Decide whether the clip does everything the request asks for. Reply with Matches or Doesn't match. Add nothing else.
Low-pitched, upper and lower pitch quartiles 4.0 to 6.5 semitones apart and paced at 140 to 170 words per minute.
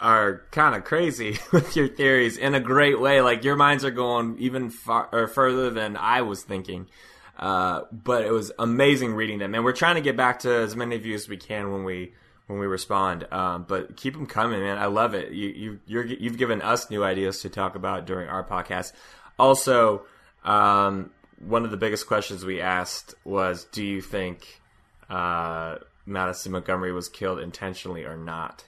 Doesn't match